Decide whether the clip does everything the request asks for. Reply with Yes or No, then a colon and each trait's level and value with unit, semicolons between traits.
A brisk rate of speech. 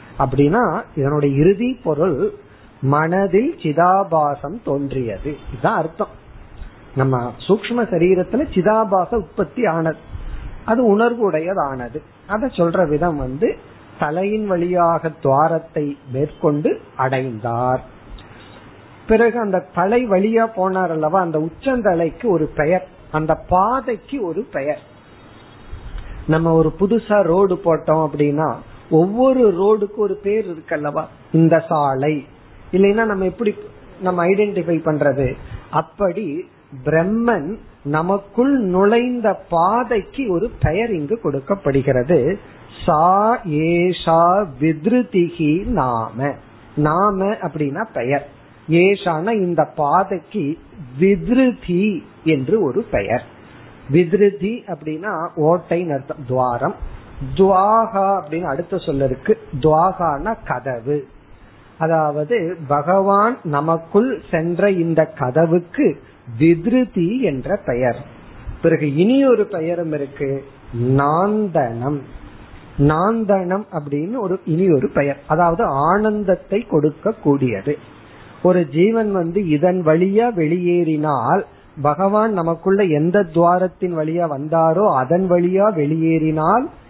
No: average, 85 wpm